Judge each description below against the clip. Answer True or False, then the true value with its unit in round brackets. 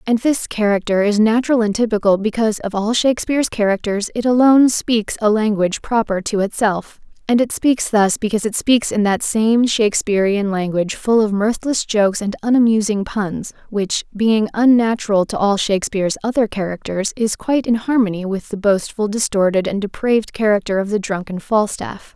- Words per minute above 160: True (170 wpm)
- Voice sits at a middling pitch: False (215 Hz)